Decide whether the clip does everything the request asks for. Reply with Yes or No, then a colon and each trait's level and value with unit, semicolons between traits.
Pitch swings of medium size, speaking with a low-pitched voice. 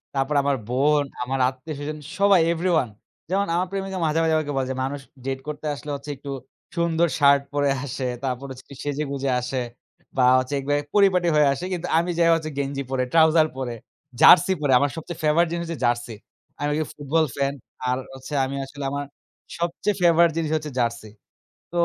No: average, 3.5 semitones; medium, 145 Hz